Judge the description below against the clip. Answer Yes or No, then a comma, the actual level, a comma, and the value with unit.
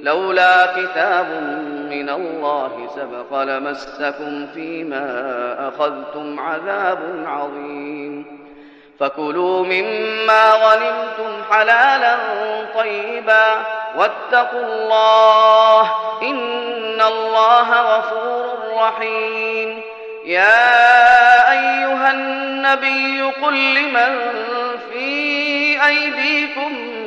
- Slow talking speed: Yes, slow, 60 wpm